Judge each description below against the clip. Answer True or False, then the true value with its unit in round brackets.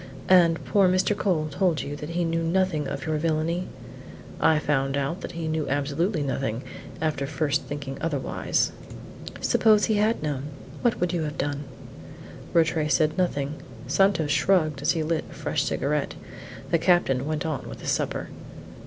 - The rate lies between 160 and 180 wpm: True (165 wpm)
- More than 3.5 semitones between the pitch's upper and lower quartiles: False (3.2 semitones)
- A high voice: False (155 Hz)